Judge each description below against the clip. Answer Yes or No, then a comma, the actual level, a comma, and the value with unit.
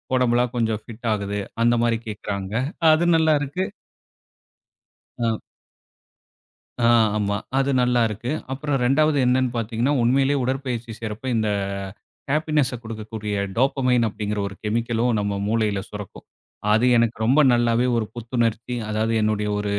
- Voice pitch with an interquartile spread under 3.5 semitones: Yes, average, 3.1 semitones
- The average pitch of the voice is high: No, low, 115 Hz